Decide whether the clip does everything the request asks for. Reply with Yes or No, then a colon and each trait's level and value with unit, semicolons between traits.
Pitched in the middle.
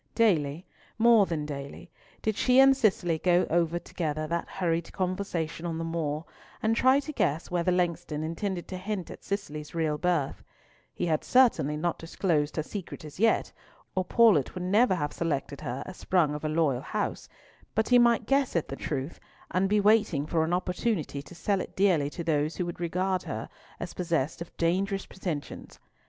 Yes: medium, 175 Hz